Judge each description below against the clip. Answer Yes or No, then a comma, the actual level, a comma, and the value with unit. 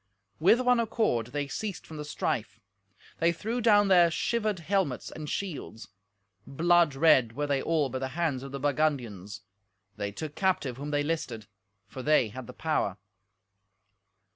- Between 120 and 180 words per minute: Yes, average, 160 wpm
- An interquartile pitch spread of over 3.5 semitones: Yes, average, 5.1 semitones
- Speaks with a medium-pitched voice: Yes, medium, 150 Hz